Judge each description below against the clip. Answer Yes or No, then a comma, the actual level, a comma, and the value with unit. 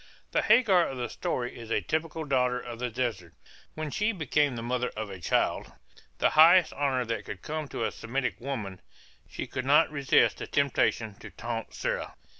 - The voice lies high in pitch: No, low, 130 Hz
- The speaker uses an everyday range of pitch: Yes, average, 4.5 semitones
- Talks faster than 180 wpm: Yes, average, 190 wpm